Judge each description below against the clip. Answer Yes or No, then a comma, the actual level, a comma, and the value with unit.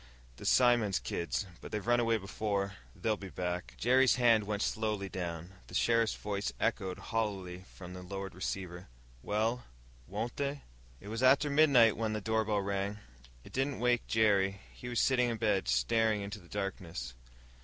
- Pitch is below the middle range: Yes, low, 105 Hz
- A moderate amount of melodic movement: Yes, average, 3.2 semitones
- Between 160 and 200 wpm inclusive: Yes, average, 165 wpm